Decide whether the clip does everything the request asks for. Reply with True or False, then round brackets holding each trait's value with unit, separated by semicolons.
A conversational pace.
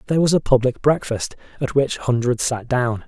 True (195 wpm)